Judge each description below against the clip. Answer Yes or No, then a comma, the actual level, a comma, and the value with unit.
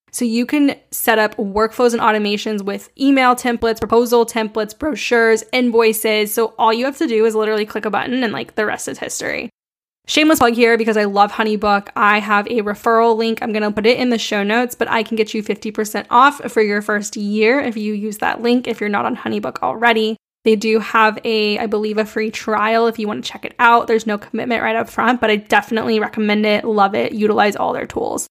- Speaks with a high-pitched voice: Yes, high, 225 Hz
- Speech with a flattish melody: Yes, narrow, 1.6 semitones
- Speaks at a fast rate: Yes, fast, 225 wpm